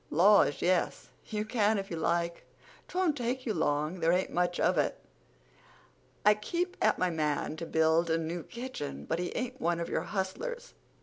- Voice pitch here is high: No, medium, 180 Hz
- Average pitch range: No, wide, 5.9 semitones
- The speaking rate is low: No, average, 175 wpm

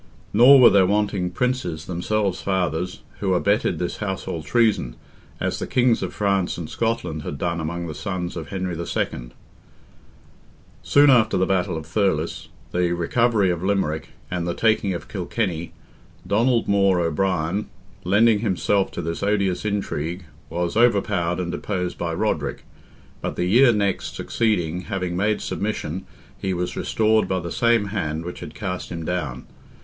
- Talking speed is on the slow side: No, average, 155 wpm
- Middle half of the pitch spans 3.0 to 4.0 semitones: Yes, average, 3.3 semitones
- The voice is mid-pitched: No, very low, 95 Hz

